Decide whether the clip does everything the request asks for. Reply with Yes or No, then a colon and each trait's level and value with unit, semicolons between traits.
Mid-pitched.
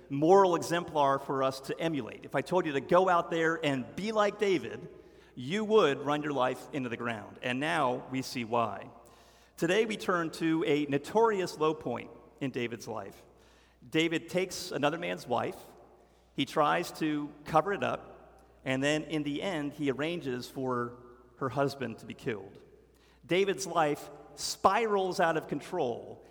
Yes: medium, 150 Hz